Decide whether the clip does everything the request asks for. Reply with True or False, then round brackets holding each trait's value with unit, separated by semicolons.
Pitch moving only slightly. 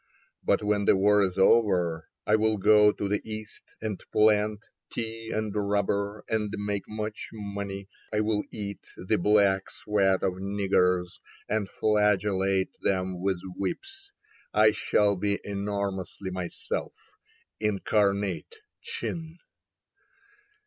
True (1.7 semitones)